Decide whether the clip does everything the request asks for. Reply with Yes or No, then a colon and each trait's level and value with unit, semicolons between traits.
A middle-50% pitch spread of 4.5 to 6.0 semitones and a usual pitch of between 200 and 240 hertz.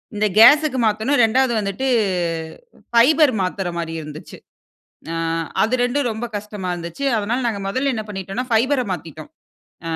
Yes: average, 5.0 semitones; high, 220 Hz